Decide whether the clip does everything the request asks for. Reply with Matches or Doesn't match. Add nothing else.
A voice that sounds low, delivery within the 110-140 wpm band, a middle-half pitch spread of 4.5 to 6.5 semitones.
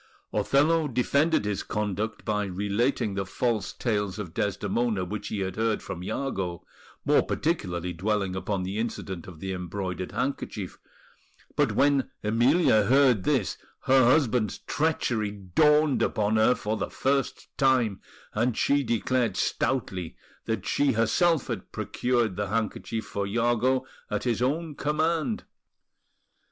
Matches